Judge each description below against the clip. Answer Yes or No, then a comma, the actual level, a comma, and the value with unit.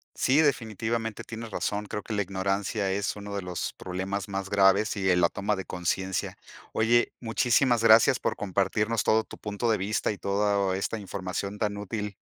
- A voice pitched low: Yes, low, 100 Hz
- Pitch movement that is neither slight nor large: No, narrow, 2.3 semitones